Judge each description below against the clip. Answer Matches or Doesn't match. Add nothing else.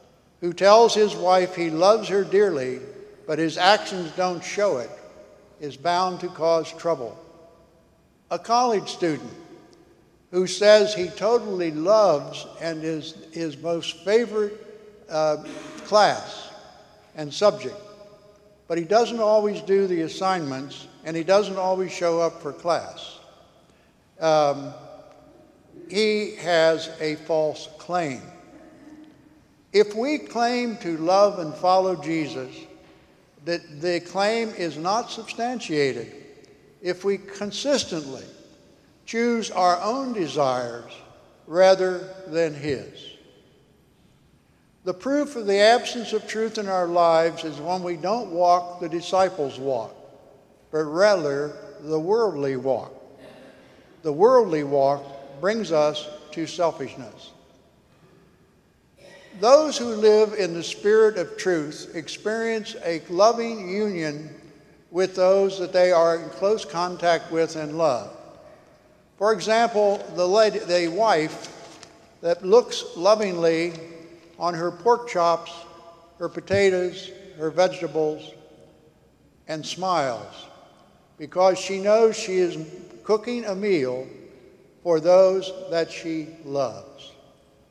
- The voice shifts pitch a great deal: Doesn't match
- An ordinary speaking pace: Doesn't match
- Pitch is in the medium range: Matches